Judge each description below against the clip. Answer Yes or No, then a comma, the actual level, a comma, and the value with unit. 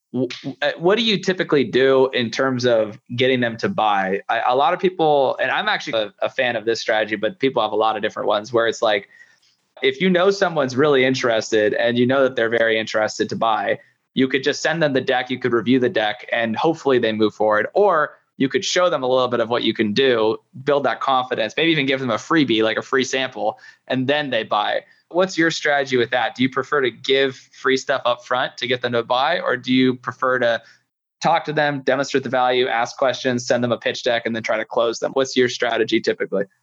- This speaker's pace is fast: Yes, fast, 240 wpm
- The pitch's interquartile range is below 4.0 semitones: Yes, average, 3.2 semitones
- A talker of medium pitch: No, low, 130 Hz